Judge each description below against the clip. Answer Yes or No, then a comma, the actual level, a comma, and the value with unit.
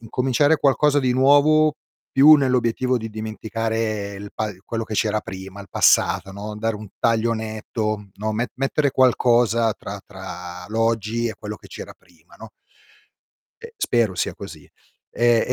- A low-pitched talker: Yes, low, 115 Hz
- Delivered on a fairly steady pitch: No, average, 3.2 semitones